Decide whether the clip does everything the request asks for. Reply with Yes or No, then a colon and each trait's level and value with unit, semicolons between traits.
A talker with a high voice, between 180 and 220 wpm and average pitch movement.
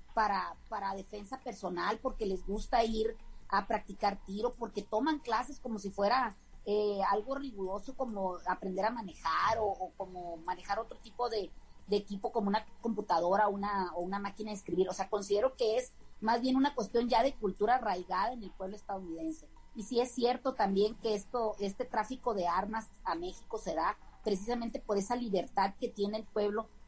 Yes: high, 210 Hz; average, 185 wpm; average, 3.3 semitones